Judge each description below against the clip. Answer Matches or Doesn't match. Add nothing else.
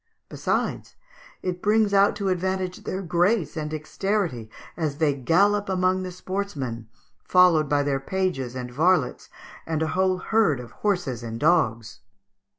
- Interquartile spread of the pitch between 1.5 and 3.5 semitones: Doesn't match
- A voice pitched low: Doesn't match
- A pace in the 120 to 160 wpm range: Matches